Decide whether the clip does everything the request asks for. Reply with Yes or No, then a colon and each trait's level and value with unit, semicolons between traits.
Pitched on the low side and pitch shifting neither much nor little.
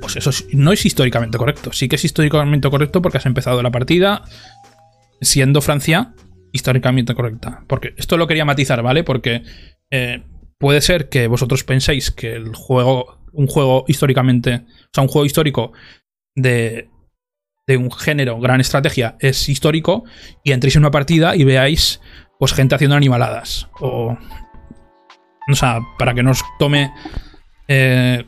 Yes: low, 130 Hz; average, 3.2 semitones